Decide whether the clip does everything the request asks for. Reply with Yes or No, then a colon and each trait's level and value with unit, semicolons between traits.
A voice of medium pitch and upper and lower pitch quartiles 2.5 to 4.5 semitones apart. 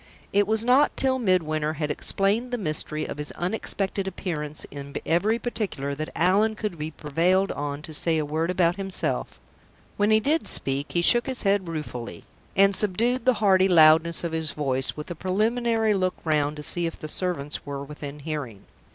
No: medium, 175 Hz; average, 5.3 semitones